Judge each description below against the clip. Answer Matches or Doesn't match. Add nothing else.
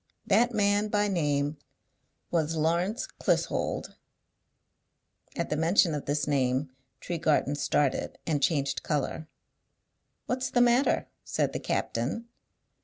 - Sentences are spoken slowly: Matches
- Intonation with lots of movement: Matches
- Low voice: Doesn't match